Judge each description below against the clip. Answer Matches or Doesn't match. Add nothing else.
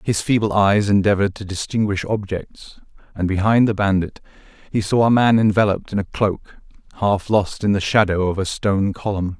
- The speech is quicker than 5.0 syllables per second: Matches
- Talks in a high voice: Doesn't match